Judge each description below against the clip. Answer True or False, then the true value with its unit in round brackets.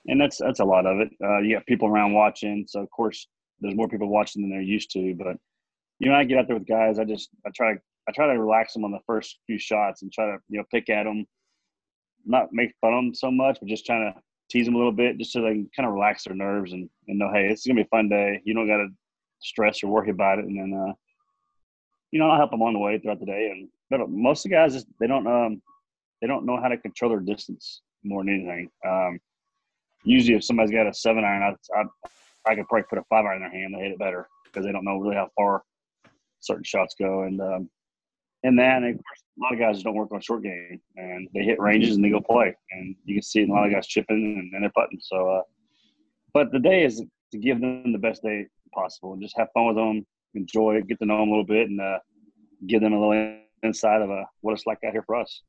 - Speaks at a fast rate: True (270 wpm)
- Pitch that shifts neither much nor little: False (2.3 semitones)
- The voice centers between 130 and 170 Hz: False (105 Hz)